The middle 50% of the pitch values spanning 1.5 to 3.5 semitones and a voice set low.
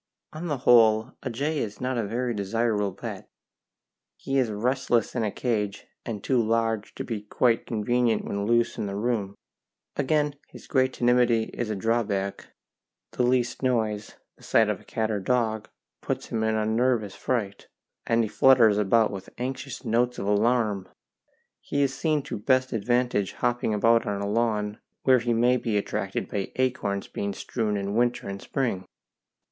Yes: average, 3.1 semitones; low, 115 Hz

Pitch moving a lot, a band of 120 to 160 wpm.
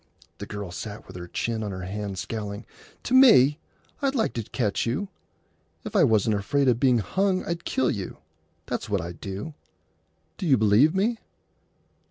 No: wide, 7.9 semitones; average, 170 wpm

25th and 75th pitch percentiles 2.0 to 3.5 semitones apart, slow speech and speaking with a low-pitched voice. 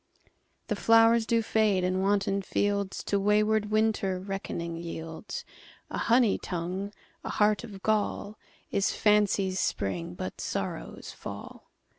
No: narrow, 2.5 semitones; slow, 110 wpm; high, 200 Hz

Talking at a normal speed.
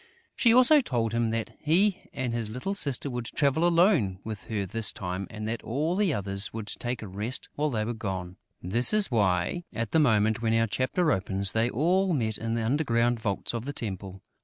No: fast, 210 wpm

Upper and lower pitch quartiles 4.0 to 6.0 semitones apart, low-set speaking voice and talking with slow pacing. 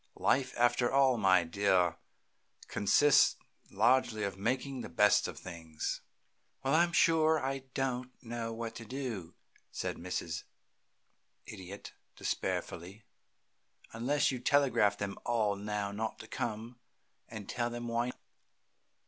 Yes: average, 4.4 semitones; low, 115 Hz; slow, 120 wpm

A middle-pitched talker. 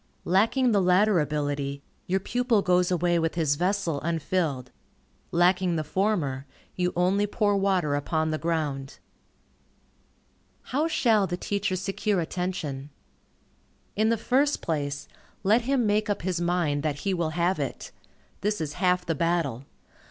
Yes: medium, 180 Hz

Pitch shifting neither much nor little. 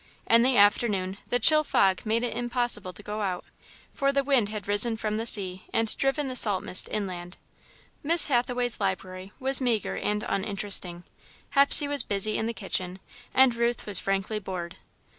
Yes: average, 4.0 semitones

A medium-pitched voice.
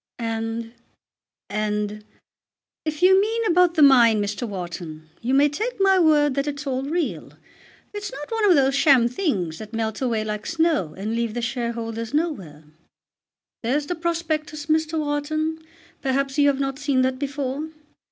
No: very high, 275 Hz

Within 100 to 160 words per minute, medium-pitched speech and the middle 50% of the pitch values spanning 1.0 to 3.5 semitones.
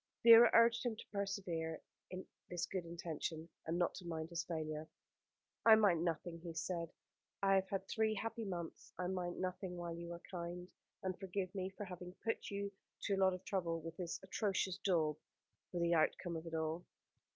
No: average, 190 wpm; medium, 180 Hz; narrow, 2.6 semitones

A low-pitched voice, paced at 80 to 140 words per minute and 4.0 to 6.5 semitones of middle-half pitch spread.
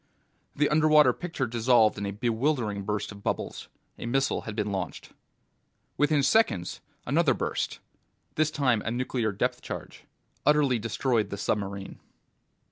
Yes: low, 120 Hz; slow, 135 wpm; wide, 5.4 semitones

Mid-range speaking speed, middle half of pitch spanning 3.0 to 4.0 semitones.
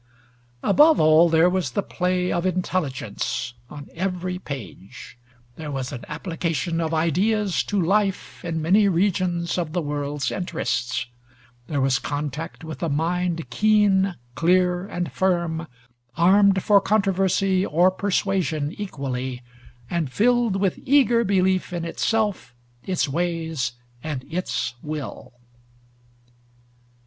No: slow, 120 wpm; average, 3.7 semitones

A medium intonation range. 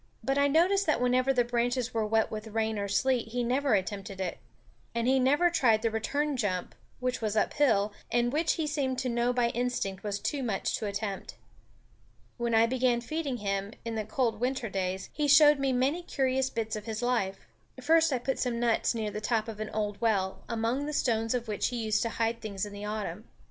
Yes: average, 3.5 semitones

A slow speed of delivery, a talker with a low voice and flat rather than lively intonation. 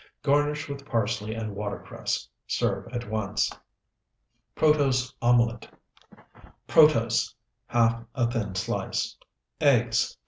No: slow, 100 wpm; low, 120 Hz; average, 4.0 semitones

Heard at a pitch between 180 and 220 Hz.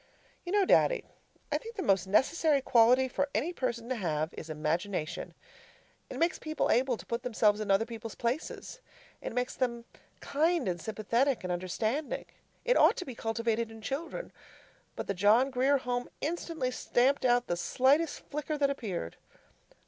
No: high, 245 Hz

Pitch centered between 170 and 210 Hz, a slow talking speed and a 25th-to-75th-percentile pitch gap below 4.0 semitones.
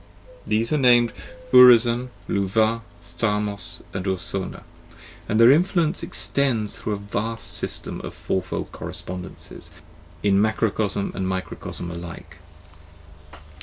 No: low, 110 Hz; slow, 105 wpm; average, 3.6 semitones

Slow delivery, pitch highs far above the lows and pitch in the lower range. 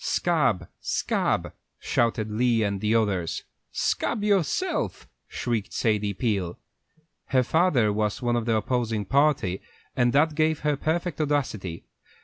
Yes: slow, 130 wpm; wide, 5.9 semitones; low, 120 Hz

